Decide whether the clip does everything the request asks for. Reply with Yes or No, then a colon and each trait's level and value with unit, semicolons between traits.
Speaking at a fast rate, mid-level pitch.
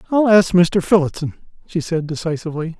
No: average, 150 wpm; medium, 170 Hz